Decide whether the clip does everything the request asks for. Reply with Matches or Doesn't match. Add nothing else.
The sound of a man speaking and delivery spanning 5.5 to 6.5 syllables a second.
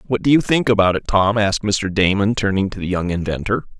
Matches